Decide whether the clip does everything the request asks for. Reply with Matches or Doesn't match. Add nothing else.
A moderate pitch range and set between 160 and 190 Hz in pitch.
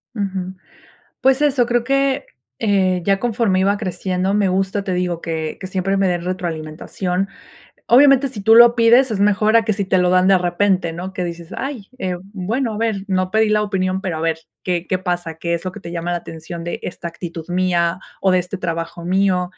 Matches